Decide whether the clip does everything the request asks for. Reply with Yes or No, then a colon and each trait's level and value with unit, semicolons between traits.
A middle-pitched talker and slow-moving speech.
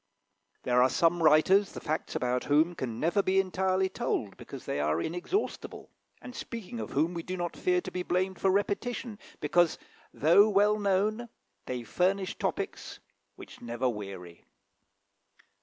No: medium, 180 Hz; average, 155 wpm